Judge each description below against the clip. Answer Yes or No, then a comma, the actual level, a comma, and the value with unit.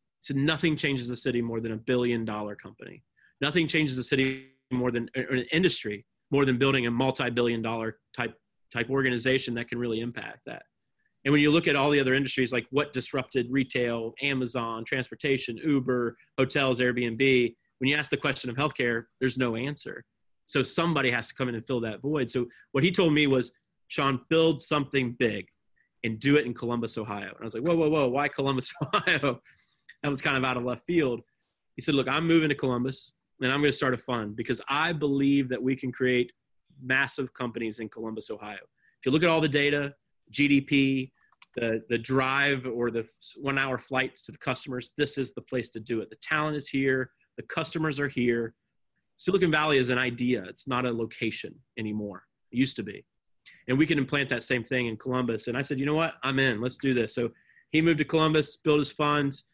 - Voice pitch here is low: Yes, low, 130 Hz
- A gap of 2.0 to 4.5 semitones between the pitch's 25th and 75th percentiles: Yes, average, 3.0 semitones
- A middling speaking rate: No, fast, 210 wpm